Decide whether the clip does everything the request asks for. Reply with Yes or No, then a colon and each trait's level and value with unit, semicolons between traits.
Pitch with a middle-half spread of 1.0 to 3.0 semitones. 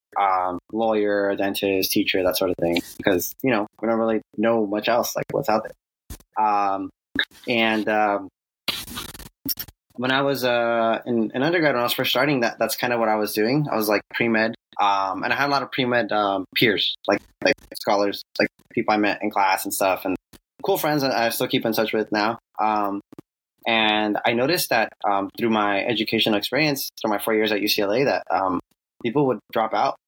Yes: narrow, 2.6 semitones